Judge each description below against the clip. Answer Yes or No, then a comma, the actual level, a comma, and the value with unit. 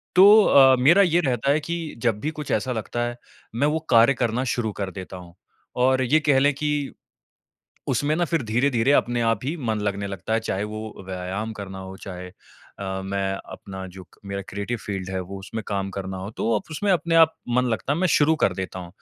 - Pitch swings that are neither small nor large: No, wide, 6.7 semitones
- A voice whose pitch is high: No, low, 115 Hz